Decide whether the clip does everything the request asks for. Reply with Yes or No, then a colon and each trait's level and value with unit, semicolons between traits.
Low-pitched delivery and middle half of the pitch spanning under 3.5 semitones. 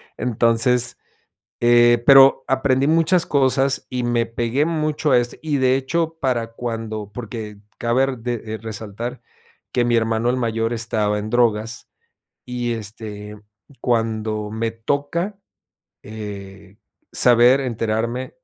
Yes: low, 120 Hz; average, 2.8 semitones